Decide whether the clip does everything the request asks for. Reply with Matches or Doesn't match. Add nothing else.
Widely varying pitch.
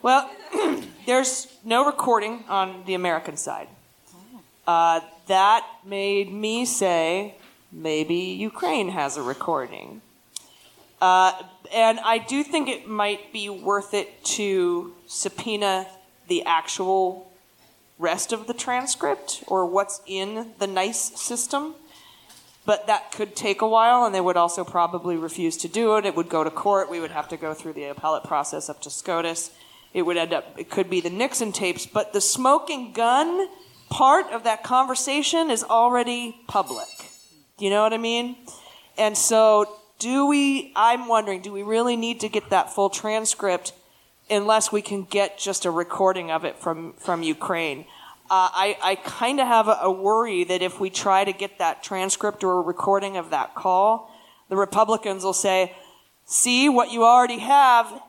Doesn't match